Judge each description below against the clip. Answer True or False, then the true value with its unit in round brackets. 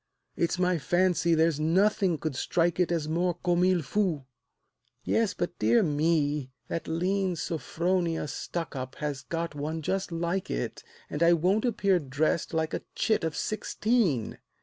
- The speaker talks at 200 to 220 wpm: False (150 wpm)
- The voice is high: False (170 Hz)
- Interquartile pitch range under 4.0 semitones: True (3.0 semitones)